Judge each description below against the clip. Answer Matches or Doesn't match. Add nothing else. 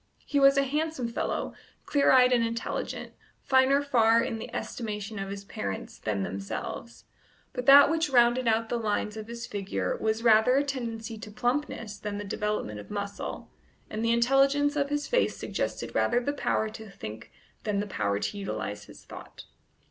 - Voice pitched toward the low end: Doesn't match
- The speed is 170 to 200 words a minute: Matches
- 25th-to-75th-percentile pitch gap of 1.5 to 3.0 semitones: Doesn't match